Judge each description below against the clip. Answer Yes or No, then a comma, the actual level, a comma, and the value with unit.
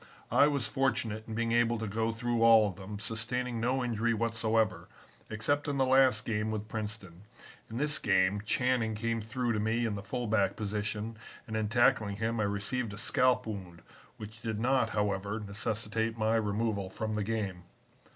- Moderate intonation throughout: No, narrow, 2.1 semitones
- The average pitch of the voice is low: Yes, low, 110 Hz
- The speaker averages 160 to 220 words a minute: Yes, average, 180 wpm